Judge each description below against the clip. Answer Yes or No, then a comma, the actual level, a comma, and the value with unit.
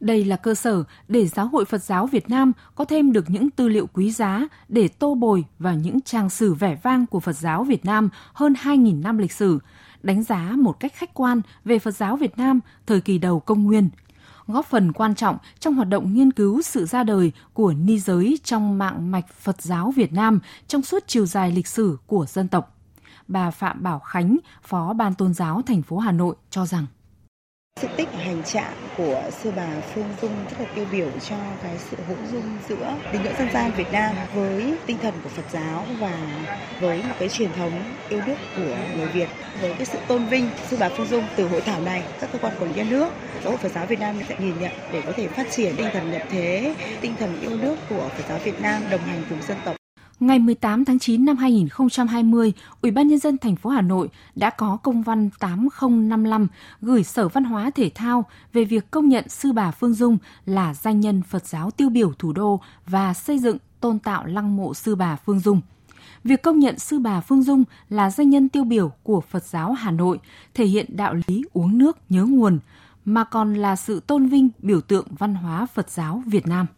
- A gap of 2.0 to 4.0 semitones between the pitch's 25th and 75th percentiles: No, average, 4.8 semitones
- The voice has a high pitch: Yes, high, 210 Hz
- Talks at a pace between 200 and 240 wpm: Yes, average, 225 wpm